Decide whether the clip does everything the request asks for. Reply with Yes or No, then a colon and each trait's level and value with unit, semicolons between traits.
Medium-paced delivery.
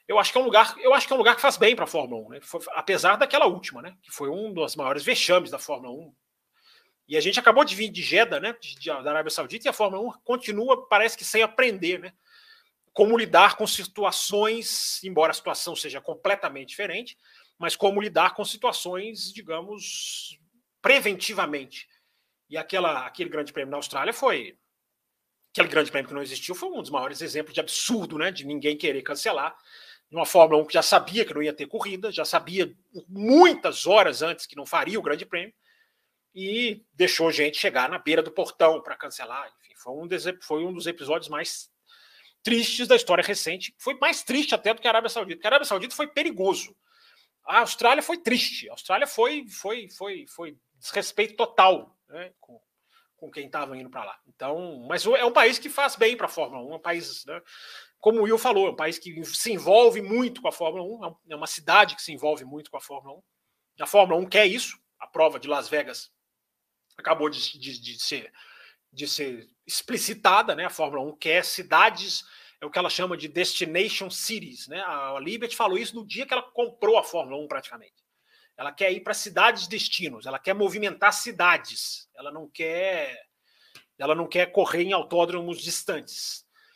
No: fast, 200 wpm